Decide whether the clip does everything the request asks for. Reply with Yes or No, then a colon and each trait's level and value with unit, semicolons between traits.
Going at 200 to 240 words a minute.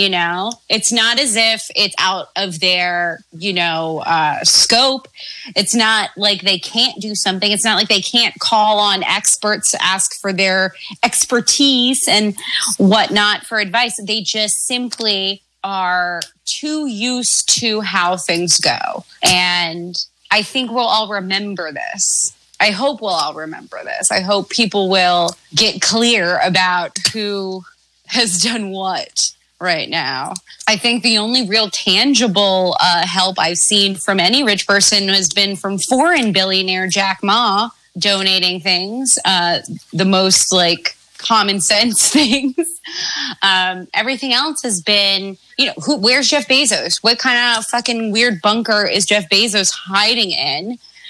No: average, 150 wpm